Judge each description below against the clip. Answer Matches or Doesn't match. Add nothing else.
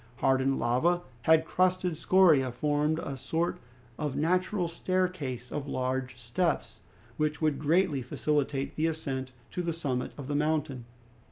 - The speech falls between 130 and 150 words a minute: Matches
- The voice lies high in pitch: Doesn't match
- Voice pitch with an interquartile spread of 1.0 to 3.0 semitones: Doesn't match